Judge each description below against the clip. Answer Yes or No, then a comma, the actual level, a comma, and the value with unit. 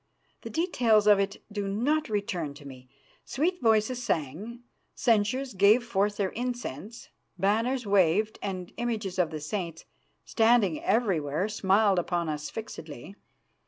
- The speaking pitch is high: Yes, high, 205 Hz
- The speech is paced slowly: Yes, slow, 130 wpm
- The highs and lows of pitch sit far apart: No, average, 4.7 semitones